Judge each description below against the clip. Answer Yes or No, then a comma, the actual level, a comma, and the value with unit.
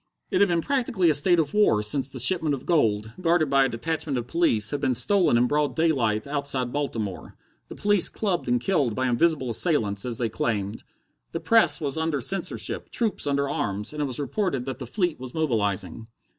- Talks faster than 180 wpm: Yes, average, 200 wpm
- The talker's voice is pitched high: No, medium, 140 Hz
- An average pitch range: No, wide, 5.8 semitones